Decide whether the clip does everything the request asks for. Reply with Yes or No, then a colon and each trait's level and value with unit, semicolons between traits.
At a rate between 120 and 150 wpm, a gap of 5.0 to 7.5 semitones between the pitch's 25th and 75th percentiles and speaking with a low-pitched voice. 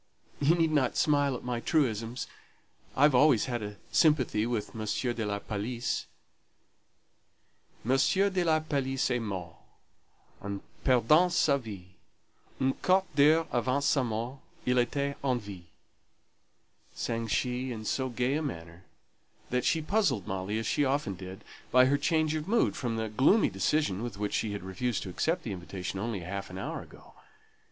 No: average, 160 wpm; wide, 5.6 semitones; low, 125 Hz